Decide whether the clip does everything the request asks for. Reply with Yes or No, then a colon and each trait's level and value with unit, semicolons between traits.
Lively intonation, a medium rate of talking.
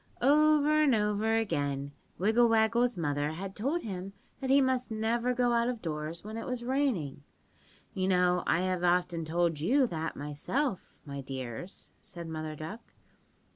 Yes: wide, 7.1 semitones; average, 160 wpm